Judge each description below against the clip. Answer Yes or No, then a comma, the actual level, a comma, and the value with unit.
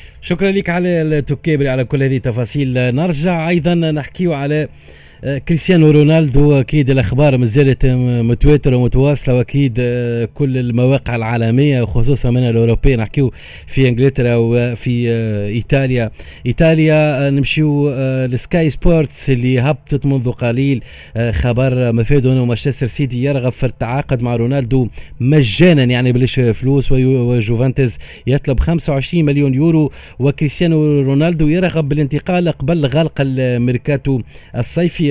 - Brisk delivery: No, average, 115 wpm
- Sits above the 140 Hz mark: No, low, 135 Hz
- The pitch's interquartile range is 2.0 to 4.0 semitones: Yes, average, 3.3 semitones